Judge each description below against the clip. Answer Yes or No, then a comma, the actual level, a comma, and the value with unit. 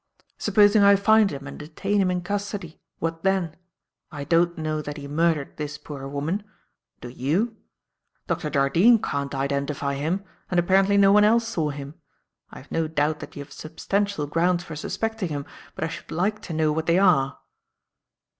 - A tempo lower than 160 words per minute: No, average, 180 wpm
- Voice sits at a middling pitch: Yes, medium, 165 Hz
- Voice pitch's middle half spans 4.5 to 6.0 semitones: Yes, average, 5.2 semitones